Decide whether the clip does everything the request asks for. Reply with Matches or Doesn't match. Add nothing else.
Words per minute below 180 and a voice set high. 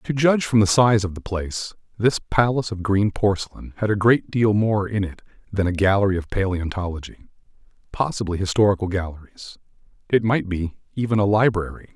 Doesn't match